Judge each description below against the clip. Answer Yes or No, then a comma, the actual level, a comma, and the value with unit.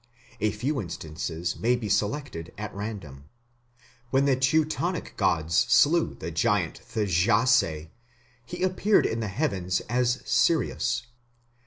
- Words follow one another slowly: Yes, slow, 120 wpm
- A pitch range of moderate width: No, wide, 7.0 semitones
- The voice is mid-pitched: No, low, 110 Hz